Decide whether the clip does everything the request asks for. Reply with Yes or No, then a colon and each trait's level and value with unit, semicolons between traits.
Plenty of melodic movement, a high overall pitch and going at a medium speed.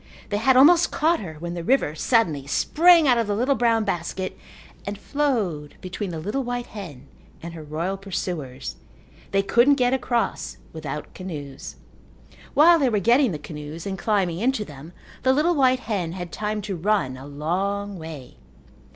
Yes: wide, 7.0 semitones; high, 195 Hz; average, 170 wpm